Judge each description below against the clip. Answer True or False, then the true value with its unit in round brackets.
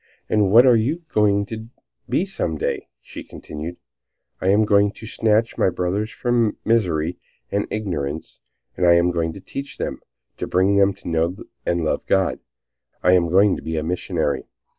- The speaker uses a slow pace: False (175 wpm)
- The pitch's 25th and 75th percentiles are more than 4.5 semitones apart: False (4.0 semitones)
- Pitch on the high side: False (95 Hz)